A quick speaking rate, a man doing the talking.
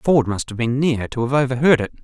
Yes: fast, 265 wpm; male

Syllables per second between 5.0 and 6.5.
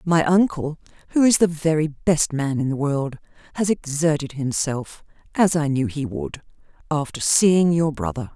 No: 4.5 syllables/s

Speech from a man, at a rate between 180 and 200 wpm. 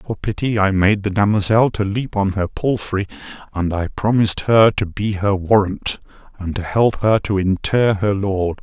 Yes: male; average, 195 wpm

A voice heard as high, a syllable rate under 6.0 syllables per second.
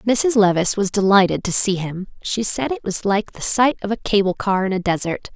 Yes: high, 205 Hz; 5.2 syllables/s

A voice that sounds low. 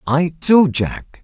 No: medium, 155 Hz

